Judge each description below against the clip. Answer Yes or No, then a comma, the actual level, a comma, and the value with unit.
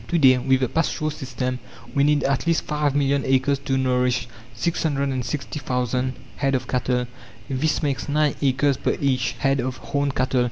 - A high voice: No, low, 135 Hz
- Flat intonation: Yes, narrow, 2.0 semitones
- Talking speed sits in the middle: Yes, average, 165 wpm